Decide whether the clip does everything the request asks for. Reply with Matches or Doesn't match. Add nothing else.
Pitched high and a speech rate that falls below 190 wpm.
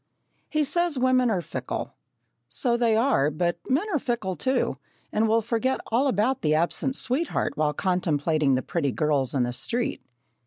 Matches